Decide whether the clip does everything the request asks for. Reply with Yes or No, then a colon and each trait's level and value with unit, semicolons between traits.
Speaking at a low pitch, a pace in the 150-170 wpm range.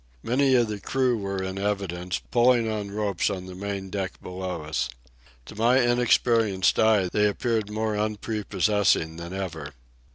Yes: low, 105 Hz; average, 155 wpm